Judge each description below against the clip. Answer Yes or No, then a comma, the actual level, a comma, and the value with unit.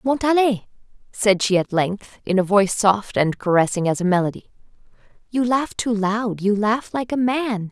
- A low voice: No, high, 210 Hz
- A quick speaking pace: No, average, 170 wpm